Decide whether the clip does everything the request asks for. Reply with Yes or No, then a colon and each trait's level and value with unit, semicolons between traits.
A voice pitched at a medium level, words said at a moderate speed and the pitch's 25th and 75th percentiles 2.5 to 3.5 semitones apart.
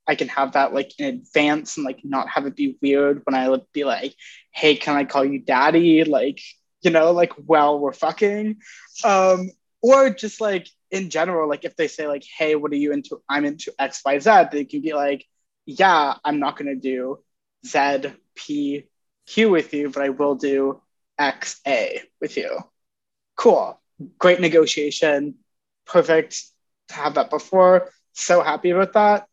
No: medium, 150 Hz; average, 180 wpm; average, 4.1 semitones